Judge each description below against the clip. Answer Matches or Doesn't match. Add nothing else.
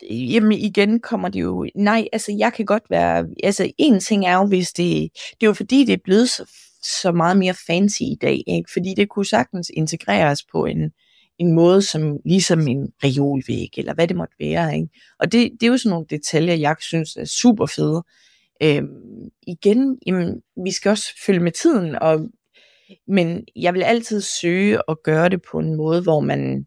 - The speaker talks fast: Doesn't match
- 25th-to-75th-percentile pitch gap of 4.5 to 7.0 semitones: Matches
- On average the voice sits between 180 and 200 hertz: Matches